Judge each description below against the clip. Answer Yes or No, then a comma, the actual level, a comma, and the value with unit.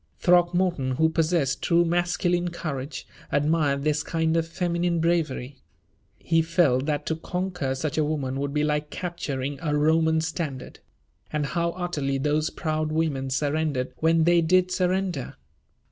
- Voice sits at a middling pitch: Yes, medium, 160 Hz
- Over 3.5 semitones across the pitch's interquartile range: No, average, 3.0 semitones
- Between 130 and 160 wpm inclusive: Yes, average, 145 wpm